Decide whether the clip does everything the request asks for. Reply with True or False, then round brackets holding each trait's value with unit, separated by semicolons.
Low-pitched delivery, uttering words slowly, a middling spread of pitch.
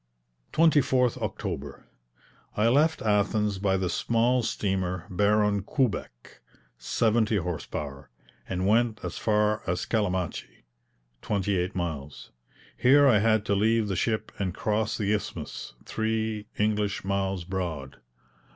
True (105 Hz; 125 wpm; 3.3 semitones)